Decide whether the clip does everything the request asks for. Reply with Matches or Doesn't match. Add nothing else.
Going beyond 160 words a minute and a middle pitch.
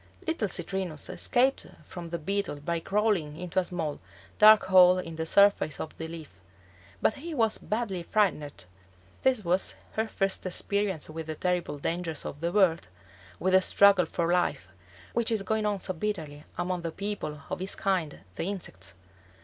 Matches